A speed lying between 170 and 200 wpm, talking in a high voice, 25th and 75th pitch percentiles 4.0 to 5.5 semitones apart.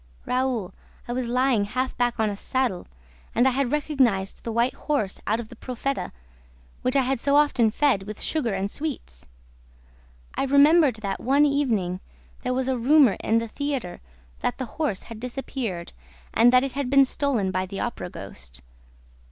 Yes: average, 175 wpm; very high, 250 Hz; average, 4.5 semitones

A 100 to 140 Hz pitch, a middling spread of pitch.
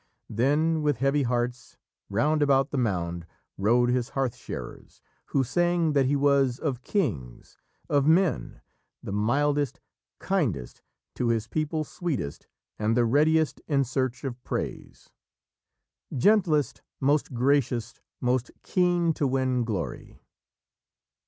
Yes: low, 135 Hz; average, 3.9 semitones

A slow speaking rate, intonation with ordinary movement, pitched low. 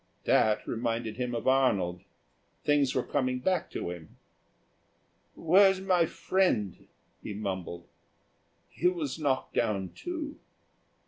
No: slow, 115 wpm; wide, 8.3 semitones; low, 130 Hz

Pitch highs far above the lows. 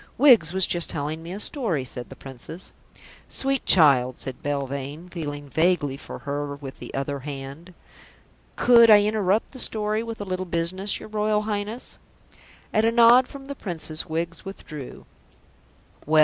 Yes: wide, 6.7 semitones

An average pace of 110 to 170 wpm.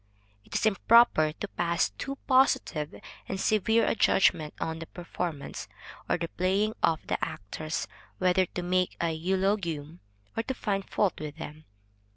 Yes: average, 155 wpm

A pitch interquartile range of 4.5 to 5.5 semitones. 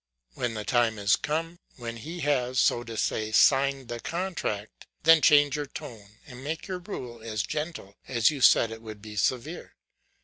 Yes: average, 5.2 semitones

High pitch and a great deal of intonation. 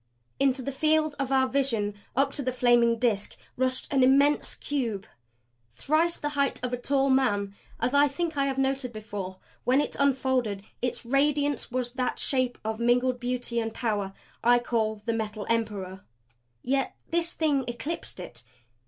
No: very high, 255 Hz; average, 3.2 semitones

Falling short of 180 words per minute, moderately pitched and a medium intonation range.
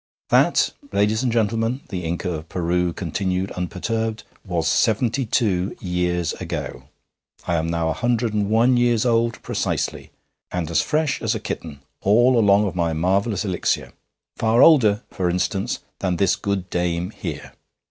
No: average, 155 wpm; low, 100 Hz; average, 4.4 semitones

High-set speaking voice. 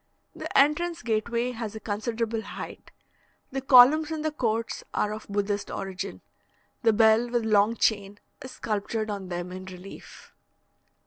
Yes: high, 220 Hz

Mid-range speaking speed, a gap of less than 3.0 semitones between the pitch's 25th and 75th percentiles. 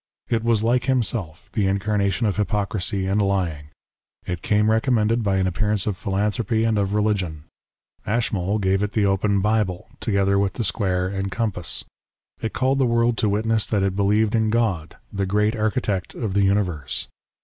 Yes: average, 175 wpm; narrow, 2.4 semitones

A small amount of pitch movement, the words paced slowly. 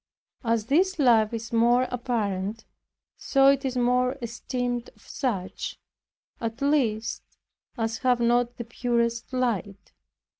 Yes: narrow, 1.9 semitones; slow, 120 wpm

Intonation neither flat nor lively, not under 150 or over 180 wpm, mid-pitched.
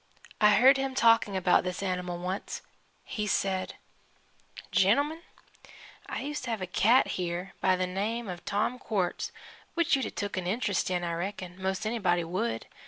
No: average, 4.0 semitones; average, 170 wpm; high, 195 Hz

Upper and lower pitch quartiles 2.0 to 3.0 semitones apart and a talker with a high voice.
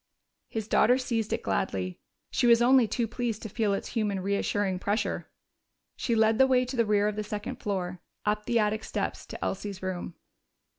Yes: average, 2.7 semitones; high, 210 Hz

